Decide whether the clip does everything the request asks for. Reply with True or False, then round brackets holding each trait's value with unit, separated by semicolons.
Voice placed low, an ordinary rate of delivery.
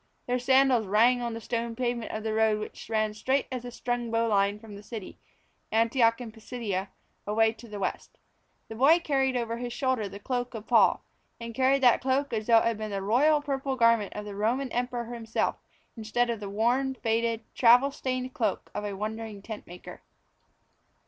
False (230 Hz; 195 wpm)